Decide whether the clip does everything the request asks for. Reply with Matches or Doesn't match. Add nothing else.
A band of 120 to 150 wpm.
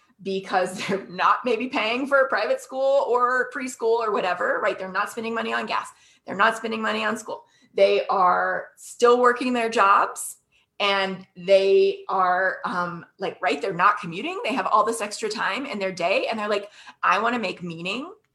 Doesn't match